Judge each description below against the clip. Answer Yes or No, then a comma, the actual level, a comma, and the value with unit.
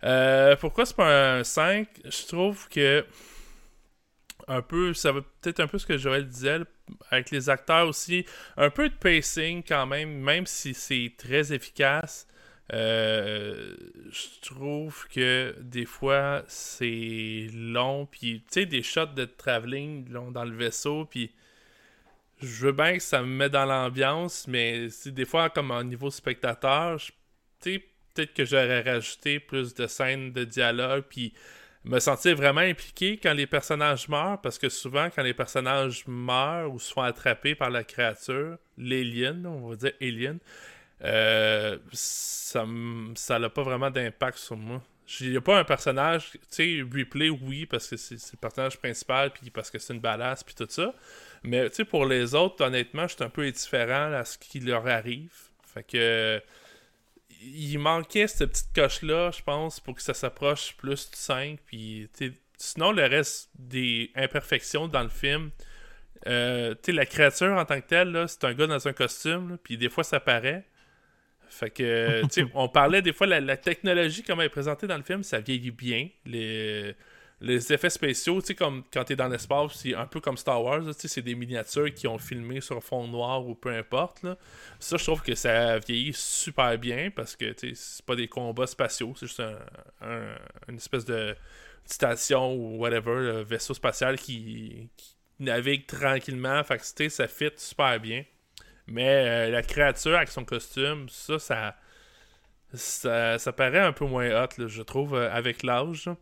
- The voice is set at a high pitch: No, low, 135 Hz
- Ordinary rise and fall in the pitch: Yes, average, 3.9 semitones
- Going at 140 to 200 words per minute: Yes, average, 180 wpm